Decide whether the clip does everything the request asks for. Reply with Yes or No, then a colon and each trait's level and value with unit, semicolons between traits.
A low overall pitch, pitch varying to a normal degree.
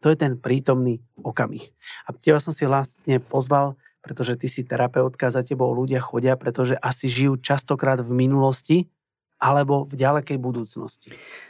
No: low, 130 Hz; narrow, 1.8 semitones